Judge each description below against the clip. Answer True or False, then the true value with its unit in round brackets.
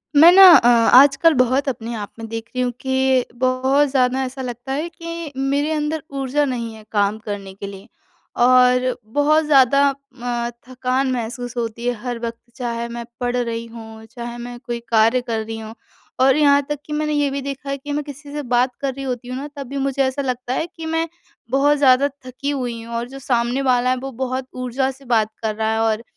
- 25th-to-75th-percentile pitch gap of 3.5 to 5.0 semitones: False (2.8 semitones)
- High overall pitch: True (255 Hz)